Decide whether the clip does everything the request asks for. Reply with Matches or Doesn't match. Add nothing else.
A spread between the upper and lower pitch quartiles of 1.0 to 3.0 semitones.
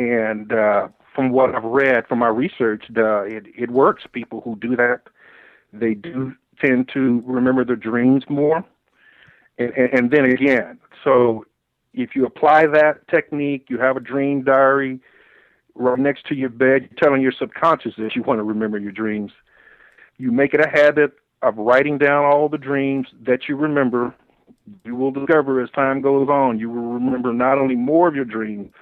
Matches